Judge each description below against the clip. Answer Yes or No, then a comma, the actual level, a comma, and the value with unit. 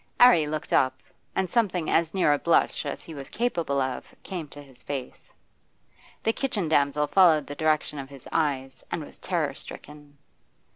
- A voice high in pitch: No, medium, 150 Hz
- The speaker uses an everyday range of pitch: Yes, average, 3.4 semitones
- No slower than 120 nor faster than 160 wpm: No, average, 175 wpm